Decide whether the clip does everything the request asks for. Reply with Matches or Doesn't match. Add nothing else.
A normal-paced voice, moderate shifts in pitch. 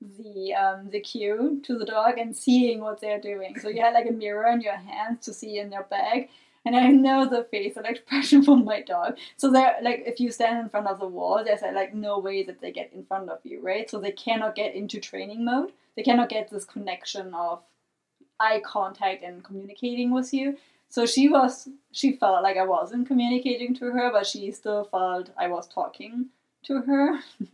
Doesn't match